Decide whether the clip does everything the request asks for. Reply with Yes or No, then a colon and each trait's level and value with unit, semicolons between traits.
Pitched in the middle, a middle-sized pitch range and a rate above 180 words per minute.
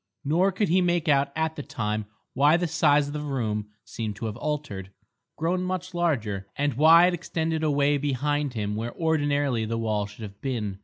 No: medium, 145 Hz; wide, 6.2 semitones; average, 195 wpm